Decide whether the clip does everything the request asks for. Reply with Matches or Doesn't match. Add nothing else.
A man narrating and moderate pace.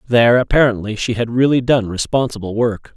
Matches